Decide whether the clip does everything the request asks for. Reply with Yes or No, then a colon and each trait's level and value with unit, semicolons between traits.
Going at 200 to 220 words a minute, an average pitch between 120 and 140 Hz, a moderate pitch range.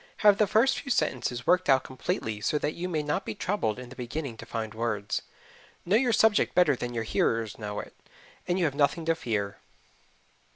No: fast, 205 wpm; low, 135 Hz; wide, 7.9 semitones